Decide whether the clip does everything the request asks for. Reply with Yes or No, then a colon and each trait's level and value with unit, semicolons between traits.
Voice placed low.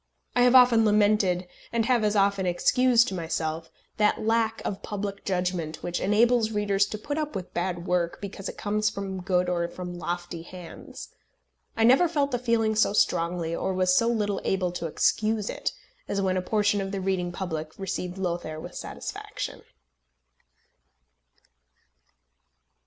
No: high, 195 Hz